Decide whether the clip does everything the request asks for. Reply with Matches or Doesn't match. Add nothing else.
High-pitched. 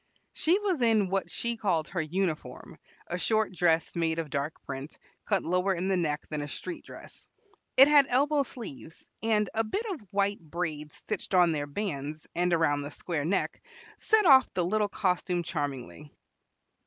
Doesn't match